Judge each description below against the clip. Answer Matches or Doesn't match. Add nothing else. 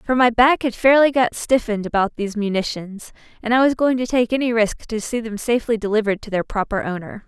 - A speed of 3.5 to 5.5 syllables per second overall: Doesn't match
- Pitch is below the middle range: Doesn't match